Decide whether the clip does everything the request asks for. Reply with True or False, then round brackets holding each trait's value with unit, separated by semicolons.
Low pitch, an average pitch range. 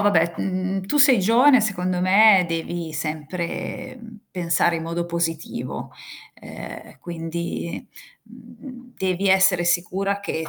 False (180 Hz; 3.0 semitones)